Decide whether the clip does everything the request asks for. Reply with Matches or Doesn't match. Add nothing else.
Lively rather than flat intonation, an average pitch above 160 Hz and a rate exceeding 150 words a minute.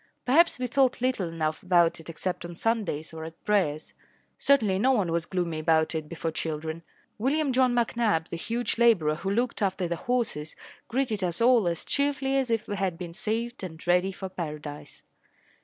Matches